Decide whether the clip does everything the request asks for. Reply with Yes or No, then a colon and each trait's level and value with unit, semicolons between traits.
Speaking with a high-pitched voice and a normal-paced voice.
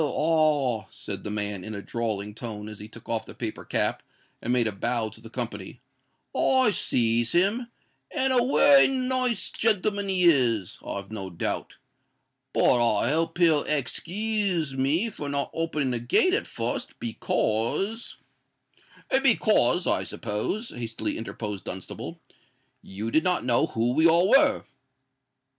No: low, 135 Hz; average, 150 wpm